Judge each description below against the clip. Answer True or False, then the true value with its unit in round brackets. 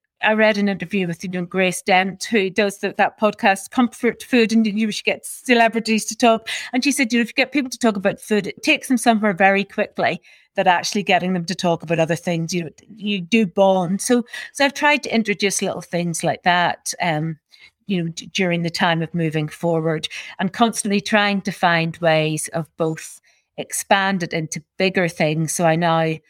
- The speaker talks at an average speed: False (210 wpm)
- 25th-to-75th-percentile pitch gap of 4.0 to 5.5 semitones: True (4.3 semitones)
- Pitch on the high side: True (195 Hz)